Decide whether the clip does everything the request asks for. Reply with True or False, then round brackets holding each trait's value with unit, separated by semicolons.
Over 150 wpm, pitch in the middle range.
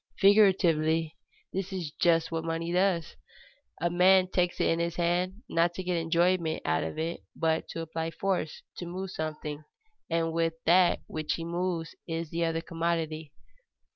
True (160 wpm; 170 Hz)